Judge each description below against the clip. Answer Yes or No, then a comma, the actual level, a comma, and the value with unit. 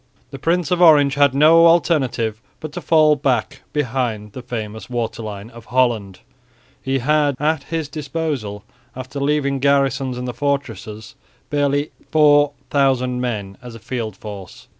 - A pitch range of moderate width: Yes, average, 4.2 semitones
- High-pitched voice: No, low, 135 Hz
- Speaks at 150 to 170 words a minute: No, average, 140 wpm